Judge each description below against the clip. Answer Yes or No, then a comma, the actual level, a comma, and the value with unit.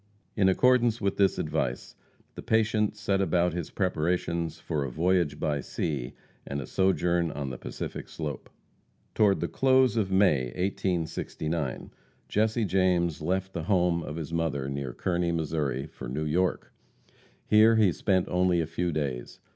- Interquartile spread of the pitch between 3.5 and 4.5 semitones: Yes, average, 4.0 semitones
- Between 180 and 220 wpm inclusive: No, average, 155 wpm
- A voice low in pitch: Yes, very low, 85 Hz